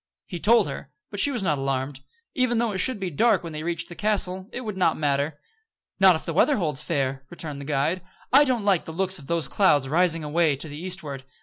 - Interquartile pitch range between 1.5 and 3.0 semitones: No, average, 4.9 semitones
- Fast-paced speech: Yes, fast, 235 wpm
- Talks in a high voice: No, medium, 170 Hz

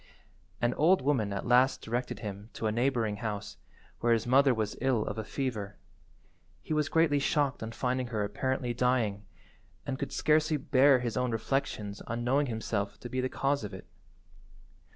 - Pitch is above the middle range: No, low, 125 Hz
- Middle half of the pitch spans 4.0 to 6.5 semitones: No, average, 3.6 semitones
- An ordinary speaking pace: Yes, average, 175 wpm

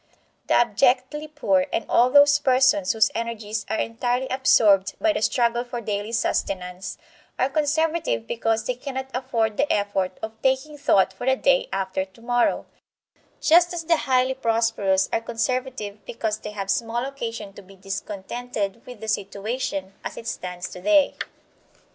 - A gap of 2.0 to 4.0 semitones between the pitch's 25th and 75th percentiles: No, average, 4.5 semitones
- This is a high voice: Yes, high, 230 Hz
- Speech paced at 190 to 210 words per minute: No, average, 155 wpm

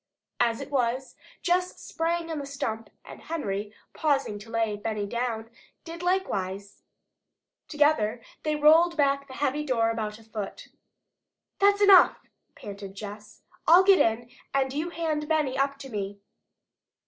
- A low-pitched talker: No, very high, 265 Hz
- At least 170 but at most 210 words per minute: No, average, 145 wpm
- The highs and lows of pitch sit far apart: Yes, wide, 6.3 semitones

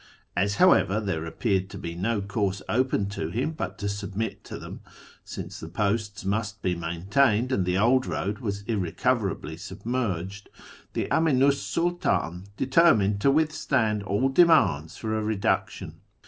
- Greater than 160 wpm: No, average, 150 wpm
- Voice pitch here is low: Yes, low, 105 Hz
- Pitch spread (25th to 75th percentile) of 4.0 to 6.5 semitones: Yes, average, 4.8 semitones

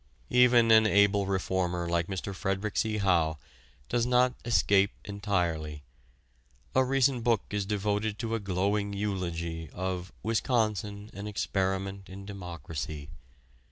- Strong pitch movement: No, average, 3.0 semitones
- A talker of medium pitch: No, low, 100 Hz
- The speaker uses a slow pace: Yes, slow, 125 wpm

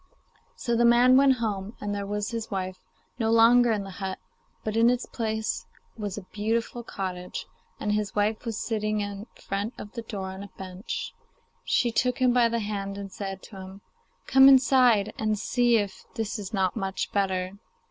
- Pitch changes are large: No, average, 2.9 semitones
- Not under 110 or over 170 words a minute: No, average, 190 wpm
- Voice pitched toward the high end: Yes, high, 210 Hz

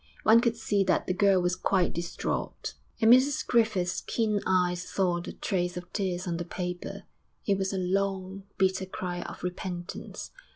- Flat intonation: Yes, narrow, 2.0 semitones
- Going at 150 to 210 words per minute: Yes, average, 170 wpm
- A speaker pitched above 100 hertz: Yes, medium, 185 Hz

